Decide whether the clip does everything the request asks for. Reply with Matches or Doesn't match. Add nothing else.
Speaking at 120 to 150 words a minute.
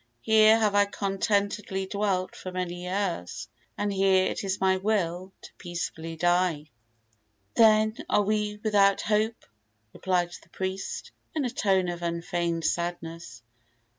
Matches